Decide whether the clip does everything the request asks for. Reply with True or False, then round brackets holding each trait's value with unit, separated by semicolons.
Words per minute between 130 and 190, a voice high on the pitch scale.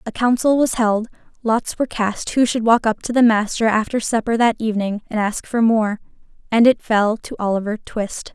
False (200 wpm; 225 Hz)